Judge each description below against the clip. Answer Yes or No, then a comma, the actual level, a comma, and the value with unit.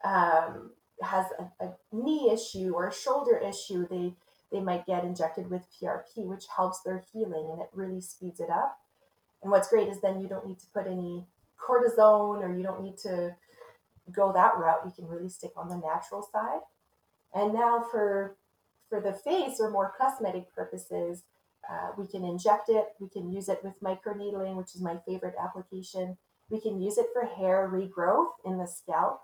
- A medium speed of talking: Yes, average, 185 wpm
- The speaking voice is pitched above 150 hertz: Yes, high, 190 Hz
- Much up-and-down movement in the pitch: No, average, 2.7 semitones